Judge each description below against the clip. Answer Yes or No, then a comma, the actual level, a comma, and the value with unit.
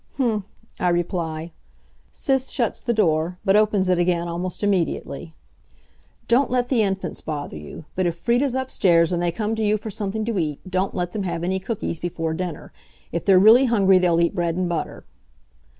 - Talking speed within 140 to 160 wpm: No, average, 185 wpm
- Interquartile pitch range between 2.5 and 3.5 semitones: No, average, 4.0 semitones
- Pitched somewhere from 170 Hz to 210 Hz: Yes, medium, 185 Hz